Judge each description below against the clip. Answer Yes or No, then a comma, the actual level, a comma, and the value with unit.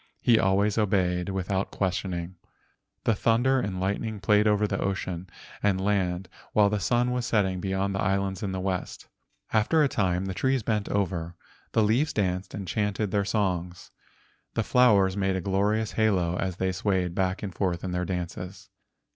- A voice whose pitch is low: Yes, very low, 95 Hz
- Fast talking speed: No, average, 170 wpm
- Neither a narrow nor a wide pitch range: No, narrow, 2.3 semitones